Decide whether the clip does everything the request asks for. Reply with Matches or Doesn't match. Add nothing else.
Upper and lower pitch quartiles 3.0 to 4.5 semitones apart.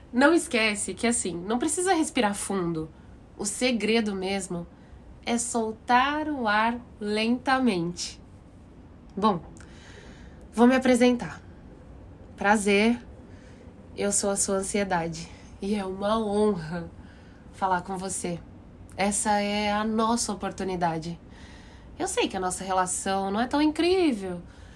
Doesn't match